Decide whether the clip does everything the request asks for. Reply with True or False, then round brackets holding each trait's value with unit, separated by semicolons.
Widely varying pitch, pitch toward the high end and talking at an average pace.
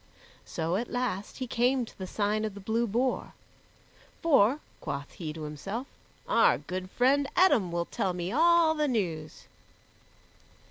True (6.1 semitones; 215 Hz; 150 wpm)